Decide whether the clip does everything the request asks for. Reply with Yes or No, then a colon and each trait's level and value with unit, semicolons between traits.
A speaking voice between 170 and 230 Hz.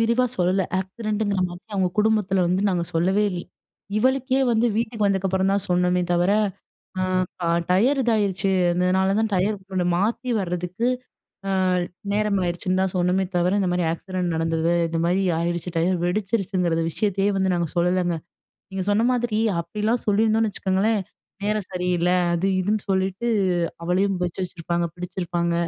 Yes: high, 190 Hz